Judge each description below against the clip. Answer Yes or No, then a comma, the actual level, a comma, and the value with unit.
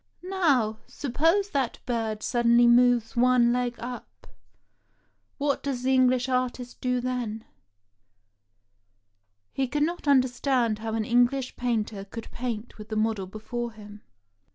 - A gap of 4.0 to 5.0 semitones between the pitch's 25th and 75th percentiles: No, average, 2.8 semitones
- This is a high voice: Yes, high, 240 Hz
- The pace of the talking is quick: No, slow, 135 wpm